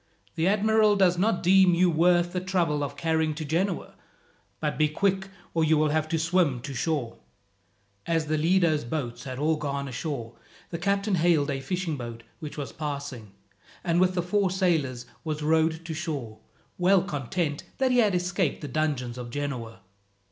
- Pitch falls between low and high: Yes, medium, 160 Hz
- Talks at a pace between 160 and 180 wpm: Yes, average, 175 wpm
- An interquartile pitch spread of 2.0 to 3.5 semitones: No, average, 3.9 semitones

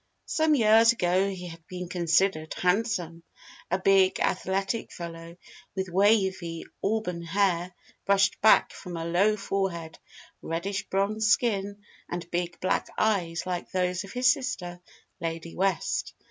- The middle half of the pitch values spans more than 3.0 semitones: No, average, 2.7 semitones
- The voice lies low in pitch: No, medium, 185 Hz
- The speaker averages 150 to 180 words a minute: No, slow, 135 wpm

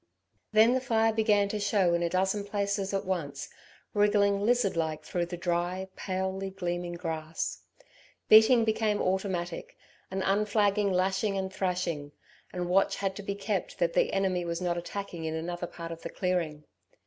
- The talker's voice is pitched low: No, high, 190 Hz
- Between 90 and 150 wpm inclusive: No, average, 165 wpm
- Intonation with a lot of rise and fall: No, average, 2.8 semitones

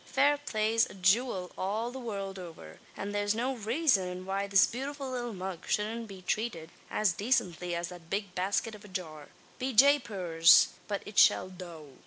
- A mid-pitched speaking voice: No, high, 200 Hz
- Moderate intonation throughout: Yes, average, 4.5 semitones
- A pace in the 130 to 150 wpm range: No, average, 175 wpm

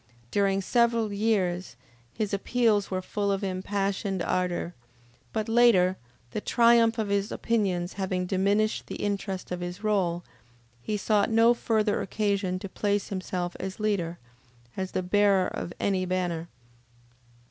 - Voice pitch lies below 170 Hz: No, high, 200 Hz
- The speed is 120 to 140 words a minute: Yes, slow, 135 wpm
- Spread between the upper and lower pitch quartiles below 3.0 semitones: Yes, narrow, 2.5 semitones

